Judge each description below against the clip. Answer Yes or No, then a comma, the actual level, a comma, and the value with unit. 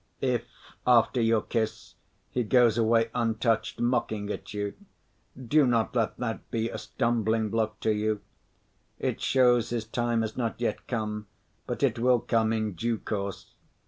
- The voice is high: No, low, 115 Hz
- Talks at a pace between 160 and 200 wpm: No, average, 150 wpm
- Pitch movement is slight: Yes, narrow, 1.7 semitones